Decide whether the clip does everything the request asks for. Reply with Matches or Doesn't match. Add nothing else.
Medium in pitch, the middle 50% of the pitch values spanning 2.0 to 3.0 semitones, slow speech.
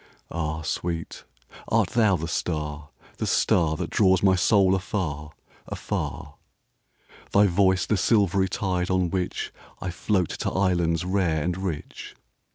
Doesn't match